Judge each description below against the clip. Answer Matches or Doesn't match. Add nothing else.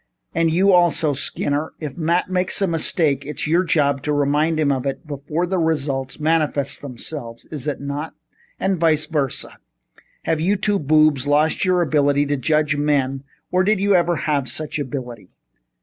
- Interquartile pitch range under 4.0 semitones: Matches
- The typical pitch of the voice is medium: Matches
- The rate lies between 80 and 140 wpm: Doesn't match